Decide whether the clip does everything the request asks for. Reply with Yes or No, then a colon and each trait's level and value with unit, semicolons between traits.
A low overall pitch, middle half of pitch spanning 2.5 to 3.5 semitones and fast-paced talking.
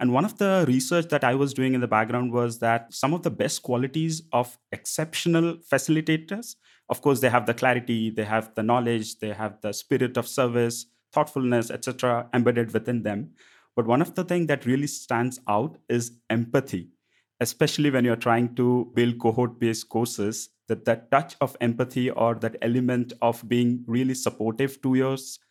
No: low, 125 Hz; average, 2.8 semitones; average, 180 wpm